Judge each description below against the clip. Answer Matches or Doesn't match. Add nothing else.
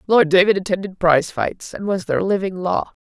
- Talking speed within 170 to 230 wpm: Matches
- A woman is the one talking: Matches